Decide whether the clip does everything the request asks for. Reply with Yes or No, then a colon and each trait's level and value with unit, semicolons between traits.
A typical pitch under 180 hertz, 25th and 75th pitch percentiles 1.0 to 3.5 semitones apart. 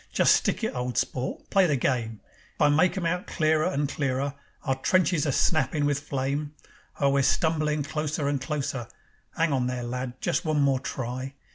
Yes: medium, 140 Hz; average, 2.9 semitones